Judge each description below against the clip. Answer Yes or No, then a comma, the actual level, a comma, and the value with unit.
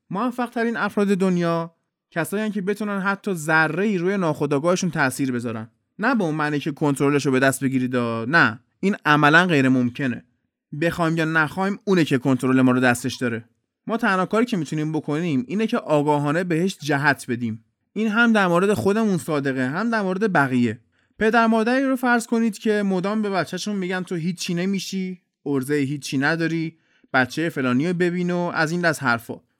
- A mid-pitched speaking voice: Yes, medium, 165 Hz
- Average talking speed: No, fast, 170 wpm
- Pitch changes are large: Yes, wide, 6.2 semitones